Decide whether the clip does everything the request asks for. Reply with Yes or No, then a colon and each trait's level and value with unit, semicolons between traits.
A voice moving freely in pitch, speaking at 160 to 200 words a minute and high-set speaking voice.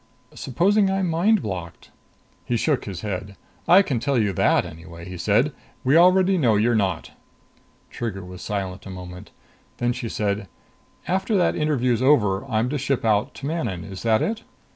No: wide, 7.8 semitones; average, 170 wpm; low, 115 Hz